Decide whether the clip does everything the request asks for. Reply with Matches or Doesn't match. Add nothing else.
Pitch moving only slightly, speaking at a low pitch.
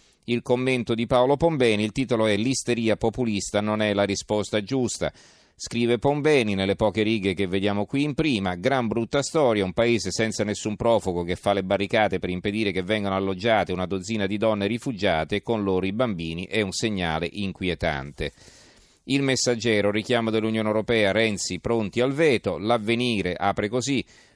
Doesn't match